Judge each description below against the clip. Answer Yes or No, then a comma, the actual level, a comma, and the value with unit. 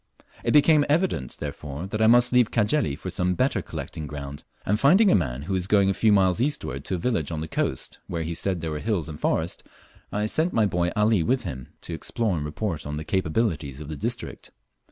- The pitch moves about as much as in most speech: No, wide, 6.6 semitones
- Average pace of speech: No, fast, 225 wpm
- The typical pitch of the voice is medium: No, very low, 95 Hz